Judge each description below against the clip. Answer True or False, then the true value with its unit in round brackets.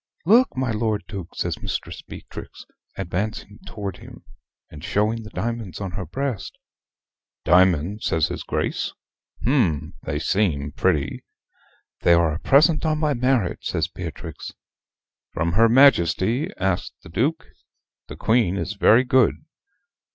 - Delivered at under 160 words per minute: True (135 wpm)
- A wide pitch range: True (6.0 semitones)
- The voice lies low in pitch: True (105 Hz)